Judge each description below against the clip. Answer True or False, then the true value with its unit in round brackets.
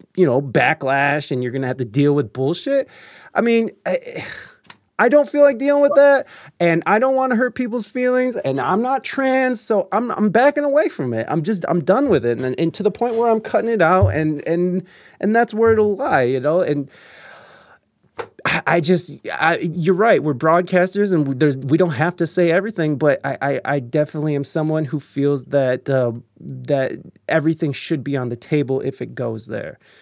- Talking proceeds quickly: True (210 wpm)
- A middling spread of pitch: False (8.2 semitones)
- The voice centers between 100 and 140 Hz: False (165 Hz)